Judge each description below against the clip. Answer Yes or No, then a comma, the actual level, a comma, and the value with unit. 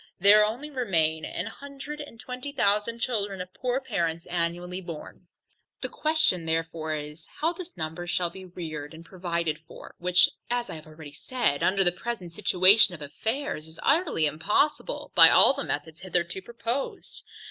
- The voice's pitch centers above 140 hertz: Yes, medium, 185 Hz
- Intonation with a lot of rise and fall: Yes, wide, 6.5 semitones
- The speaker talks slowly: No, average, 165 wpm